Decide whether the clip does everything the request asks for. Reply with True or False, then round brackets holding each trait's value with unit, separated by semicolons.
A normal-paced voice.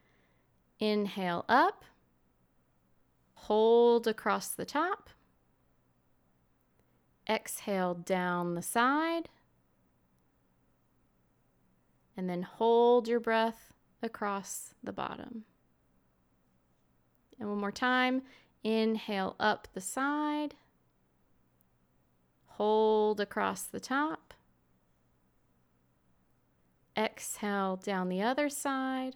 False (70 wpm)